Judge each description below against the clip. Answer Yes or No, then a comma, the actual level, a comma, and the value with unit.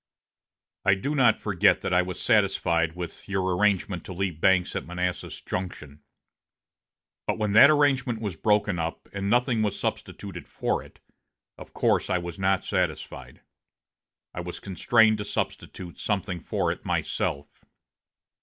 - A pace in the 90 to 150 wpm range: Yes, average, 145 wpm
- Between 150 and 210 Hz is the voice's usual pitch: No, very low, 95 Hz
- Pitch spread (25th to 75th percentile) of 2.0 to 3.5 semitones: Yes, average, 3.2 semitones